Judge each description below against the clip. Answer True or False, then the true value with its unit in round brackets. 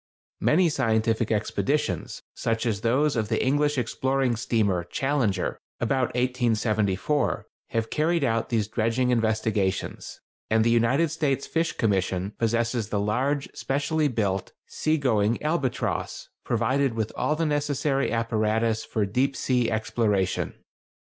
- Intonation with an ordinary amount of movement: True (4.1 semitones)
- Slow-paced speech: True (125 wpm)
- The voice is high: False (115 Hz)